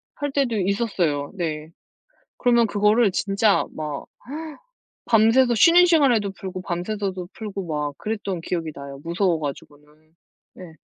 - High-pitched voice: Yes, high, 195 Hz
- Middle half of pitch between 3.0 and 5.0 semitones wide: No, wide, 5.4 semitones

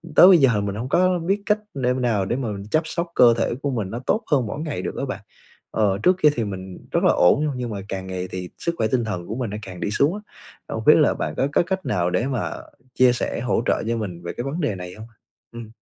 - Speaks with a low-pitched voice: Yes, low, 120 Hz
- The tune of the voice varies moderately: No, wide, 6.1 semitones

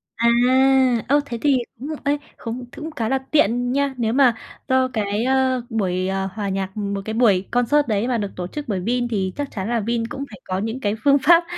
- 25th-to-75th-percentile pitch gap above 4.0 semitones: Yes, average, 4.5 semitones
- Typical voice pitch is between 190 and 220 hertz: No, high, 235 Hz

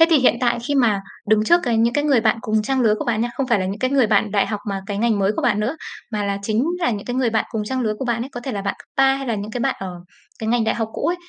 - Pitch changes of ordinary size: Yes, average, 3.4 semitones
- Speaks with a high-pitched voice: Yes, high, 230 Hz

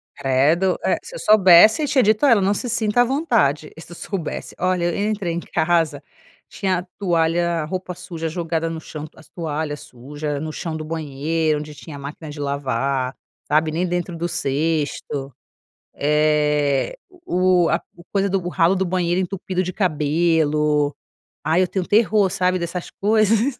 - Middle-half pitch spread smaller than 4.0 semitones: Yes, average, 3.6 semitones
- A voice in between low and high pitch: Yes, medium, 170 Hz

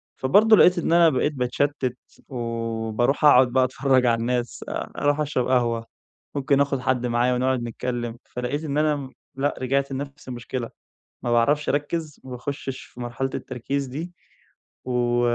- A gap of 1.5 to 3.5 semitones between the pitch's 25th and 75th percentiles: Yes, average, 2.8 semitones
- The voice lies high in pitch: No, low, 130 Hz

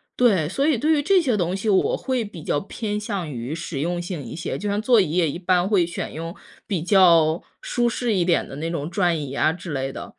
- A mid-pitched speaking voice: Yes, medium, 180 Hz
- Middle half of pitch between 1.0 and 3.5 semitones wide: No, average, 4.5 semitones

